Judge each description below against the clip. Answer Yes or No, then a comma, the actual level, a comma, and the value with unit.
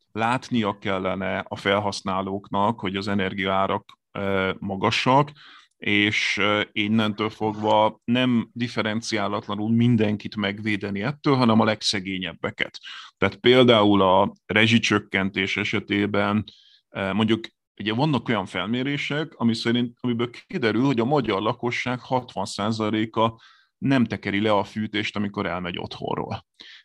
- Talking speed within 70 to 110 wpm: Yes, slow, 105 wpm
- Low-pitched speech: Yes, low, 105 Hz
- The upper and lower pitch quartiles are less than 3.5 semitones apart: Yes, average, 2.8 semitones